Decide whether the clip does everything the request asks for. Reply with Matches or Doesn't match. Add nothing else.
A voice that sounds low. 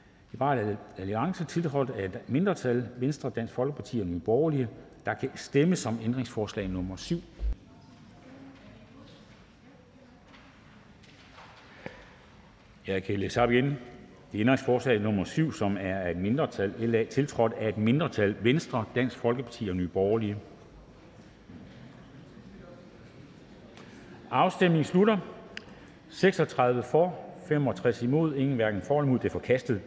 Matches